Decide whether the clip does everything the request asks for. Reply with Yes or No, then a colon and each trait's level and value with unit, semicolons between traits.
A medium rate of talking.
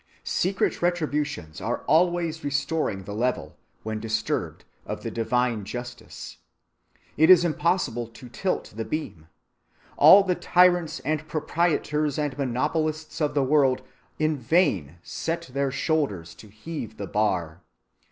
No: slow, 130 wpm